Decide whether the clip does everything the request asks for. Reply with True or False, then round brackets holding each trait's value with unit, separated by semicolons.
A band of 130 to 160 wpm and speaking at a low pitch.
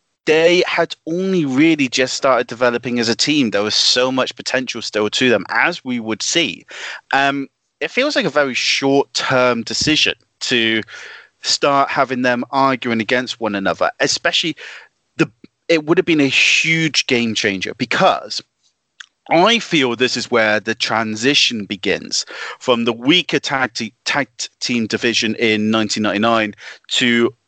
True (150 wpm; 125 Hz)